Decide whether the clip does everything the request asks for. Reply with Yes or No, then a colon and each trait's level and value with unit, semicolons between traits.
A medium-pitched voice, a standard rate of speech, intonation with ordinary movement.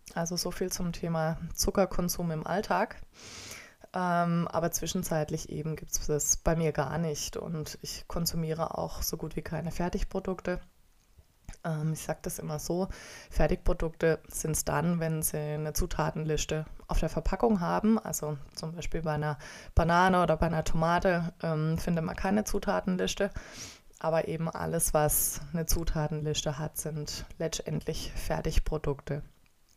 No: medium, 160 Hz; average, 145 wpm; narrow, 2.3 semitones